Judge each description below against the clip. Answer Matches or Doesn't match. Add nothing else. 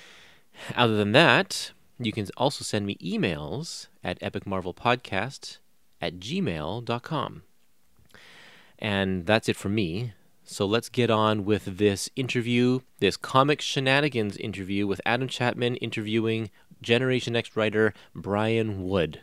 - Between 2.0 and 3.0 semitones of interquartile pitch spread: Doesn't match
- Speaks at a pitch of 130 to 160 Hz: Doesn't match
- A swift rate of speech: Doesn't match